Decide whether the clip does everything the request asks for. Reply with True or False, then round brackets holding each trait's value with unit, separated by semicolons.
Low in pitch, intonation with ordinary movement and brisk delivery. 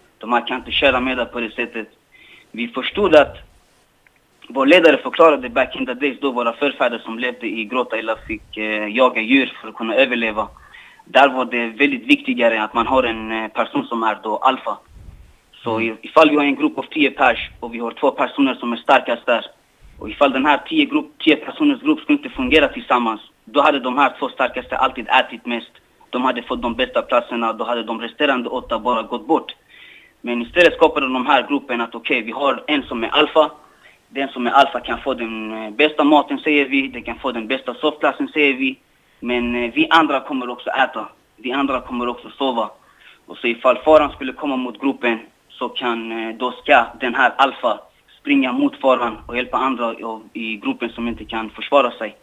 True (125 Hz; 4.1 semitones; 205 wpm)